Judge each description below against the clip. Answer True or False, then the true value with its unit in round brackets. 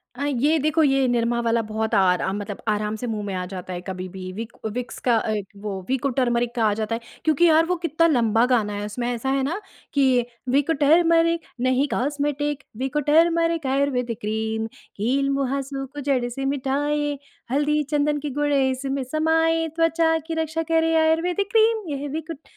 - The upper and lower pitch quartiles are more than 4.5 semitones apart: True (5.0 semitones)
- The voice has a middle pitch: False (275 Hz)